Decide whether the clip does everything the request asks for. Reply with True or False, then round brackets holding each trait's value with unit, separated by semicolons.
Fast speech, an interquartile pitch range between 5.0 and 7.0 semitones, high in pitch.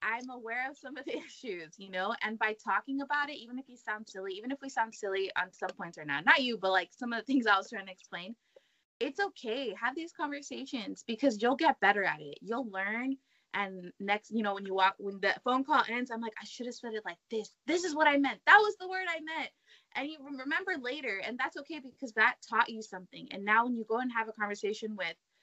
True (255 wpm; 5.3 semitones; 230 Hz)